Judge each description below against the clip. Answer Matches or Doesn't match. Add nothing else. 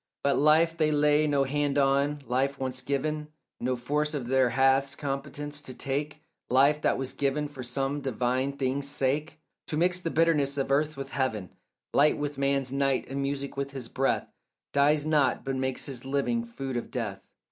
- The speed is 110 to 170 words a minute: Doesn't match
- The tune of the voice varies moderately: Doesn't match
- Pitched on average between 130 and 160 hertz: Matches